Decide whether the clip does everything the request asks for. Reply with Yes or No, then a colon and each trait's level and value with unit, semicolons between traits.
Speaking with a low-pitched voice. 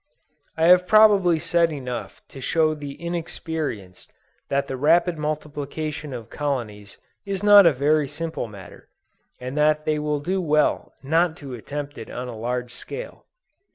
No: medium, 150 Hz